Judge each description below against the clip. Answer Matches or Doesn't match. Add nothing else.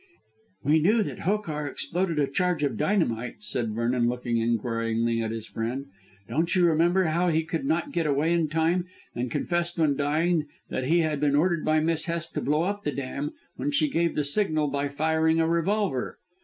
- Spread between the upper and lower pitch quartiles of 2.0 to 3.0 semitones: Doesn't match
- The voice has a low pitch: Doesn't match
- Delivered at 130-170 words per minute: Doesn't match